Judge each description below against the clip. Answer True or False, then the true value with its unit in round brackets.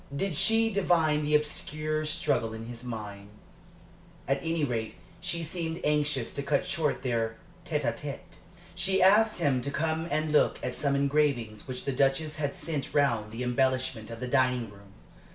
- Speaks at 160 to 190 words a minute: True (175 wpm)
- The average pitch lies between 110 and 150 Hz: True (140 Hz)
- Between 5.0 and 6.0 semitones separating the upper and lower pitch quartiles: False (4.1 semitones)